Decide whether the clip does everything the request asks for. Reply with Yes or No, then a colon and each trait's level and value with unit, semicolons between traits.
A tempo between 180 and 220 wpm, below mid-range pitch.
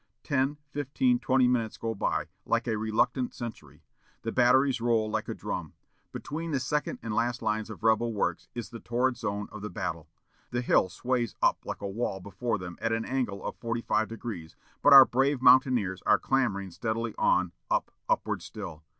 Yes: average, 185 wpm; low, 115 Hz